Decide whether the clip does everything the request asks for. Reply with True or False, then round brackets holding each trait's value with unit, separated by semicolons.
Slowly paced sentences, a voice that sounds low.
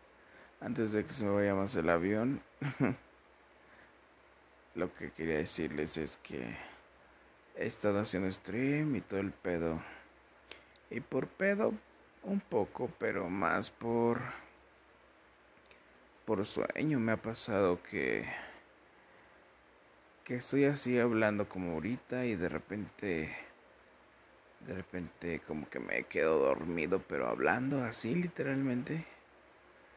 True (115 wpm; 110 Hz)